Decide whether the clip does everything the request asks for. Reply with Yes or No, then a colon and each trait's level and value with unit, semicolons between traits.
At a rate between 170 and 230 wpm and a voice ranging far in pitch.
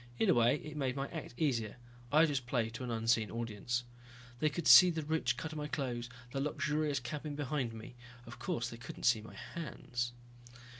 No: average, 200 wpm; average, 4.2 semitones